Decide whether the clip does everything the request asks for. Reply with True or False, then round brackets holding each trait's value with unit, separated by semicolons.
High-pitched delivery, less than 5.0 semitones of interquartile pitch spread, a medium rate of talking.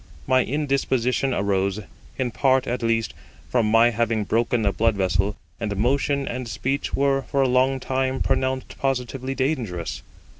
False (125 Hz; 3.4 semitones; 150 wpm)